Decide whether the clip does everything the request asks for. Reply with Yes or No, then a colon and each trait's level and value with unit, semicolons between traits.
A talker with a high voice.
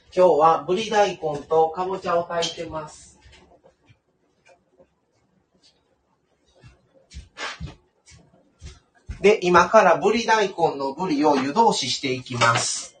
No: medium, 170 Hz